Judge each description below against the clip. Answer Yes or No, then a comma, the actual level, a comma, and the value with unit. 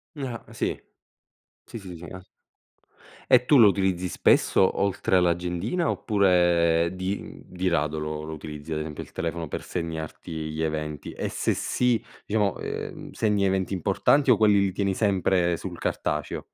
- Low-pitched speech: Yes, very low, 90 Hz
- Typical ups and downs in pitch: Yes, average, 3.7 semitones